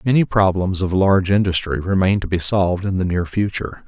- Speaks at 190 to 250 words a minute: Yes, average, 200 wpm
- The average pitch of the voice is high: No, very low, 95 Hz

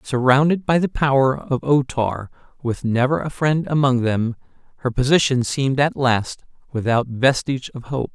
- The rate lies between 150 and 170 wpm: Yes, average, 160 wpm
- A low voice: Yes, low, 130 Hz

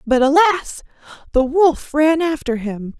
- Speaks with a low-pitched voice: No, very high, 290 Hz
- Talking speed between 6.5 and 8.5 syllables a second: No, 3.9 syllables/s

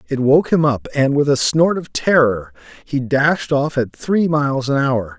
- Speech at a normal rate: No, fast, 210 wpm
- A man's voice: Yes, male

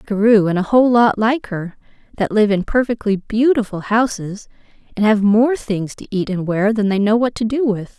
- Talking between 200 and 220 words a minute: Yes, fast, 205 wpm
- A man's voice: No, female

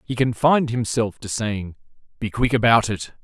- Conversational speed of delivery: Yes, average, 165 wpm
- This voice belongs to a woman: No, male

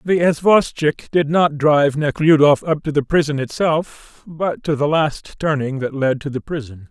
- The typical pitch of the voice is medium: Yes, medium, 150 Hz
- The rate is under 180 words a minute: No, average, 185 wpm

